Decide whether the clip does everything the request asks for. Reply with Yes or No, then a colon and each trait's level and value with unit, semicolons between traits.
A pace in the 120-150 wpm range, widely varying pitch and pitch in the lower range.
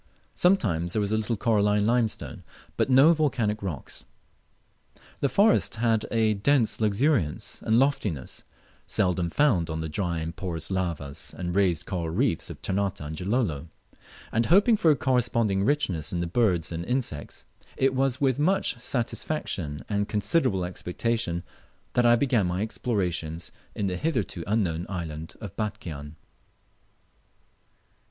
Yes: average, 145 wpm; wide, 6.1 semitones; low, 105 Hz